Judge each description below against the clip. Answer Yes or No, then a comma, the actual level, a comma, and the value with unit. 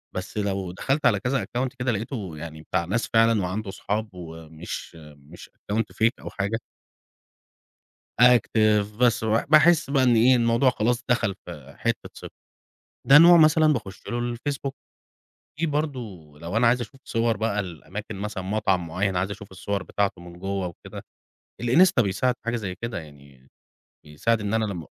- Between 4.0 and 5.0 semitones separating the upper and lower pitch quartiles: Yes, average, 4.6 semitones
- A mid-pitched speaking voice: No, low, 105 Hz